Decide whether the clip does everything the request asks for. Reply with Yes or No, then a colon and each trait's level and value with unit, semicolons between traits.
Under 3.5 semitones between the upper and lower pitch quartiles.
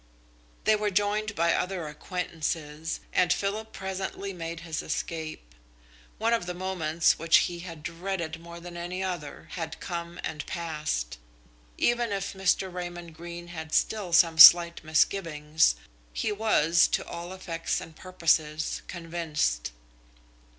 Yes: average, 2.8 semitones